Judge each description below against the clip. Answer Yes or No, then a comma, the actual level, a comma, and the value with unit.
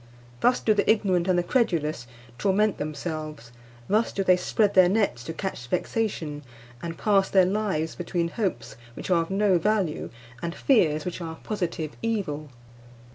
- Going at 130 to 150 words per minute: No, average, 165 wpm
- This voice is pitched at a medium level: Yes, medium, 180 Hz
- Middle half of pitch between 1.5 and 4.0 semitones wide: No, average, 4.4 semitones